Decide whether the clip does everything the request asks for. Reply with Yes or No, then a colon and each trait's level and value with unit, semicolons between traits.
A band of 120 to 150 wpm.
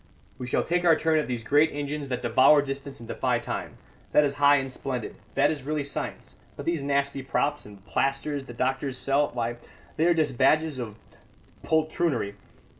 No: average, 190 wpm